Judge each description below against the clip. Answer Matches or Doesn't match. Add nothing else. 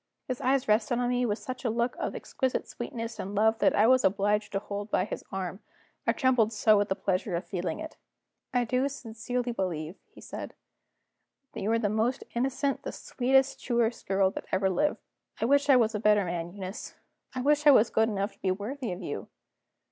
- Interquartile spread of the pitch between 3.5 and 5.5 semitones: Matches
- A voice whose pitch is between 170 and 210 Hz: Doesn't match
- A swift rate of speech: Matches